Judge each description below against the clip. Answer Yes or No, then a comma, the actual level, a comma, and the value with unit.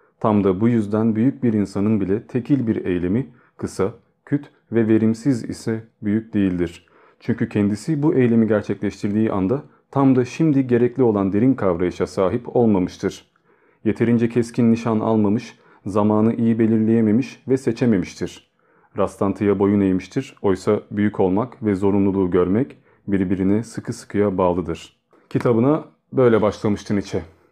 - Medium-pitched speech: No, low, 110 Hz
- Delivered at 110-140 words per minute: Yes, average, 130 wpm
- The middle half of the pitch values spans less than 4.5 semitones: Yes, average, 3.1 semitones